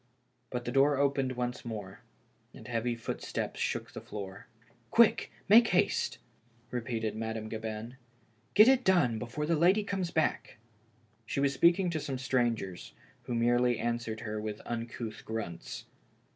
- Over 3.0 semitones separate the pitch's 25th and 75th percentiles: Yes, average, 4.2 semitones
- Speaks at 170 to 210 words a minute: No, average, 150 wpm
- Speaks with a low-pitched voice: Yes, low, 120 Hz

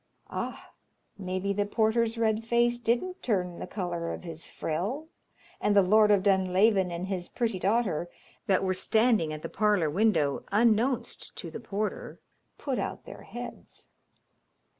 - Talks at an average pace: Yes, average, 150 wpm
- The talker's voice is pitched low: No, high, 205 Hz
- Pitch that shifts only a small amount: No, average, 3.8 semitones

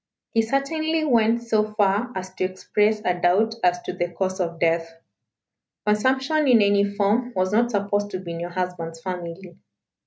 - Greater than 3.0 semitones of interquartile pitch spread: Yes, average, 4.0 semitones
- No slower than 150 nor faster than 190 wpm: Yes, average, 175 wpm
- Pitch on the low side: No, high, 200 Hz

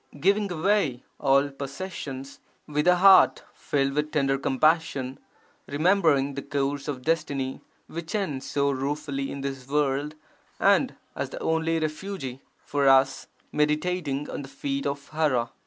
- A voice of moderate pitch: Yes, medium, 145 Hz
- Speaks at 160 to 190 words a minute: No, average, 140 wpm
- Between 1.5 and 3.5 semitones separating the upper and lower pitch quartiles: Yes, average, 3.0 semitones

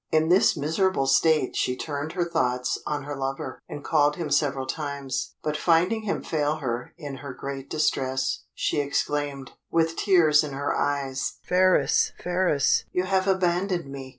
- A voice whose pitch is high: No, medium, 150 Hz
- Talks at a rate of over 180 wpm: No, average, 160 wpm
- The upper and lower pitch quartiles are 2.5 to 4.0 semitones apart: Yes, average, 3.7 semitones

